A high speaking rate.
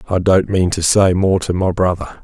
Yes: fast, 240 wpm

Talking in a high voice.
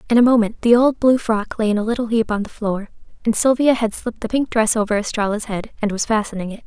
Yes: high, 225 Hz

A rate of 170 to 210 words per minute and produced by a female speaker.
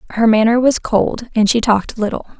Yes: average, 200 wpm; female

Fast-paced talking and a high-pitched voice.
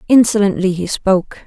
No: slow, 125 wpm; high, 195 Hz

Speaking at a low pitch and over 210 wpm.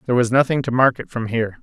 Yes: low, 120 Hz; fast, 295 wpm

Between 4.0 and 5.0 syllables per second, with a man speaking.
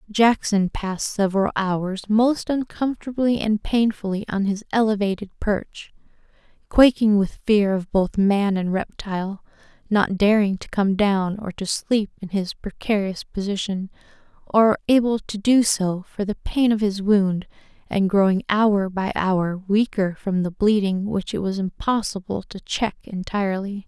No: 4.3 syllables/s; female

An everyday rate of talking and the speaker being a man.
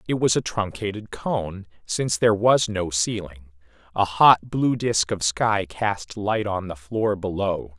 Yes: average, 170 wpm; male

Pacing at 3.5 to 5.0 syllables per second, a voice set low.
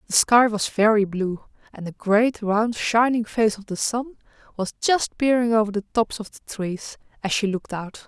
No: 4.6 syllables/s; high, 220 Hz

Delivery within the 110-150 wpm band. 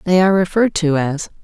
No: fast, 210 wpm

